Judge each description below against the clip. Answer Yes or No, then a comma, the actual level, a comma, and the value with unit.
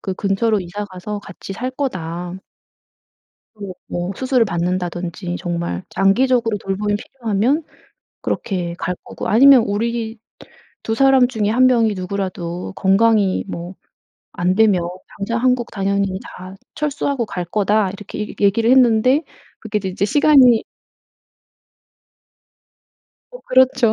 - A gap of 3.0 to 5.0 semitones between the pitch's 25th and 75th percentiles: Yes, average, 4.4 semitones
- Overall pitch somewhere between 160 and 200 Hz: No, high, 210 Hz